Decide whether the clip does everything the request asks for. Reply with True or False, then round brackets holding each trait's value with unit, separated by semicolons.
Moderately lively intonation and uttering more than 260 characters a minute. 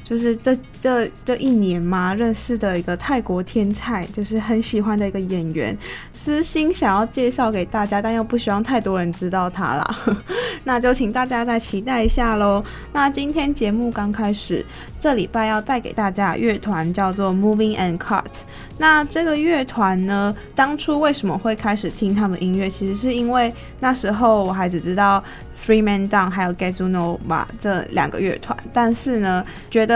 True (4.1 semitones; 310 characters per minute)